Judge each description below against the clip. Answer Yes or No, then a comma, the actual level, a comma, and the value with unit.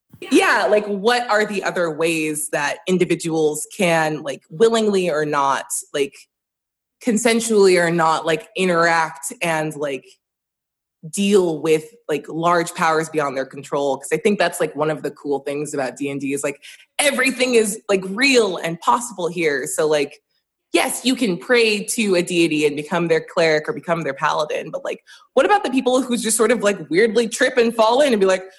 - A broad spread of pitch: Yes, wide, 6.3 semitones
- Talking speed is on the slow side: No, average, 185 wpm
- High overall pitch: No, medium, 175 Hz